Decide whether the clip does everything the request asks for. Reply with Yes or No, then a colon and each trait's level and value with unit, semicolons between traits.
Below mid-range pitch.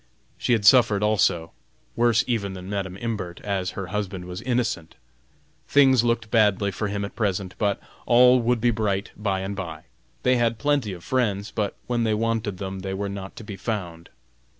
Yes: low, 105 Hz